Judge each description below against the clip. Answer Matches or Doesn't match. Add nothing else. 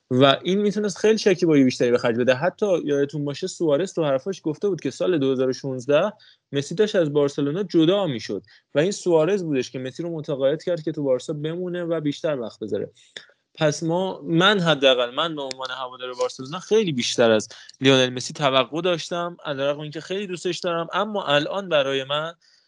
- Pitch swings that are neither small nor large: Matches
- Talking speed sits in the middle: Doesn't match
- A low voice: Doesn't match